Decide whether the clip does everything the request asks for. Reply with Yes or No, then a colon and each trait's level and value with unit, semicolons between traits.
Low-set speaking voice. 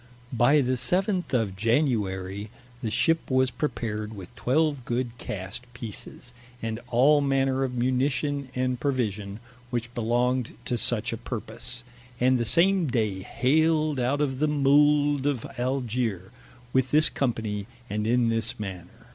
Yes: low, 125 Hz